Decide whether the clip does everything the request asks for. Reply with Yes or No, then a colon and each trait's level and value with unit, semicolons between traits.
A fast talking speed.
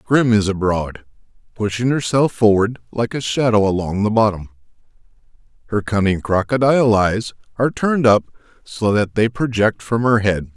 No: average, 150 wpm